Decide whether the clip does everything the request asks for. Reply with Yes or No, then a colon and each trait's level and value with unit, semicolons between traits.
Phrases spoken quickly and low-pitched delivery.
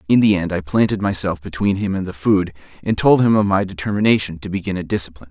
Yes: fast, 240 wpm; very low, 95 Hz